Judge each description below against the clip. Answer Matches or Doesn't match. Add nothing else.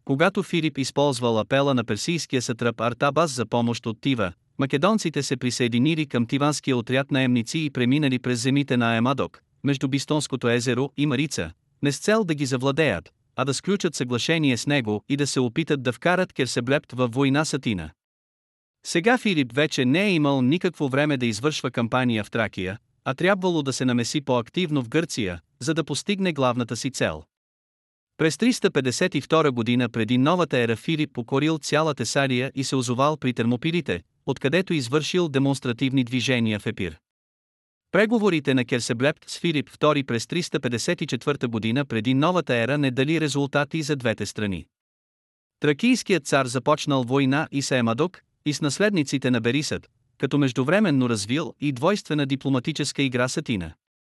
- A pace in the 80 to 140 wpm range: Doesn't match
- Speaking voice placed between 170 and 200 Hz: Doesn't match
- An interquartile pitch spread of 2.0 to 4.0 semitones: Matches